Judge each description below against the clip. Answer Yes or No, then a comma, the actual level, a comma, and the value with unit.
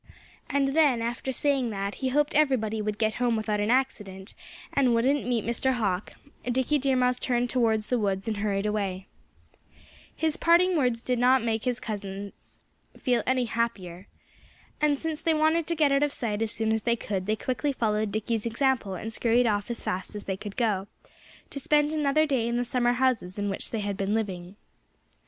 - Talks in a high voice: Yes, high, 235 Hz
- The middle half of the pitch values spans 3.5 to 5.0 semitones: Yes, average, 4.1 semitones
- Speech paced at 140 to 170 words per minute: No, average, 195 wpm